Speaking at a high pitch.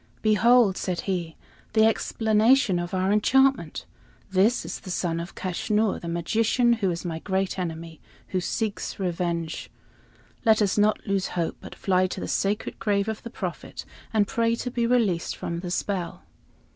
Yes: high, 195 Hz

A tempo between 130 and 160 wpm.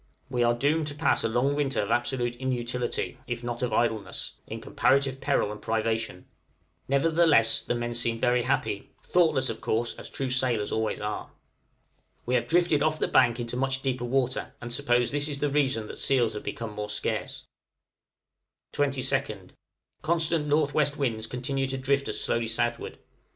No: average, 170 wpm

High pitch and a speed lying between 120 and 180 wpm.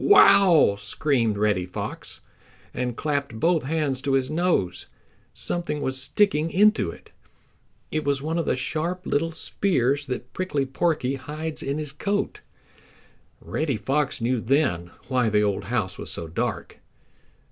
No: medium, 140 Hz; average, 145 wpm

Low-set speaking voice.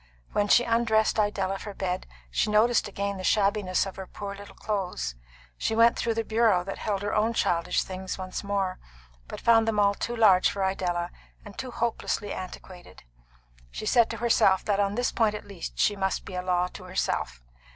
No: high, 200 Hz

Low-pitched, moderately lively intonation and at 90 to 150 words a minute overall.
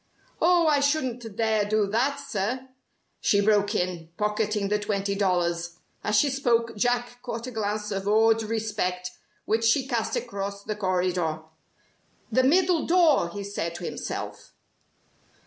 No: high, 215 Hz; average, 3.6 semitones; average, 145 wpm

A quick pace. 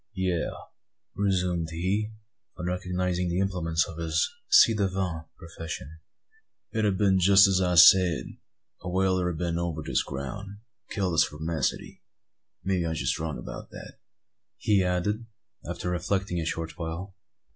No: average, 145 wpm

